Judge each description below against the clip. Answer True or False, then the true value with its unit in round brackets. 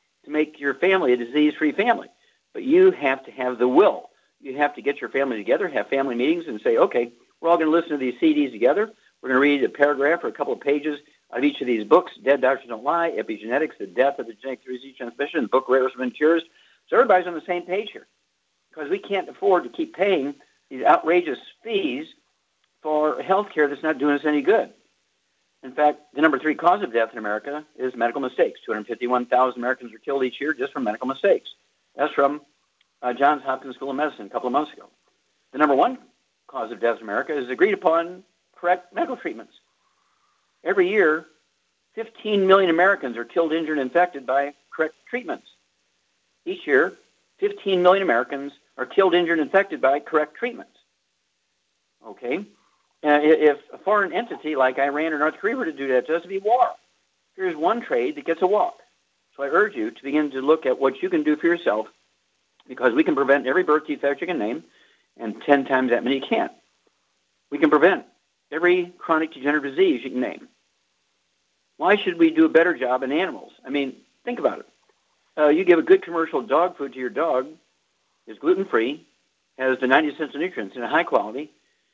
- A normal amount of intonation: False (6.7 semitones)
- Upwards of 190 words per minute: True (200 wpm)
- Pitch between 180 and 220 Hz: False (155 Hz)